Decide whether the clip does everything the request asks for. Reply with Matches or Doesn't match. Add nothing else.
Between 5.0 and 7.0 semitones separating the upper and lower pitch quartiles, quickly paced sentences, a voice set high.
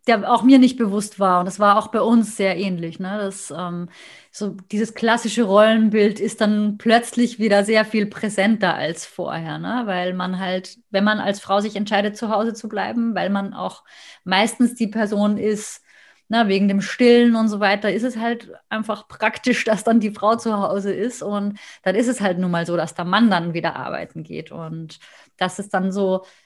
Doesn't match